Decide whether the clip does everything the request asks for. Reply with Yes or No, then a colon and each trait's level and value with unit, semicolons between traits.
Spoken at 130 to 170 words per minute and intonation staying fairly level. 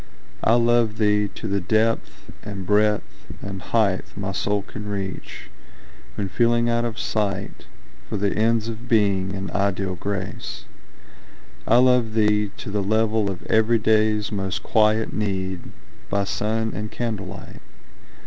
Yes: average, 140 wpm; narrow, 2.1 semitones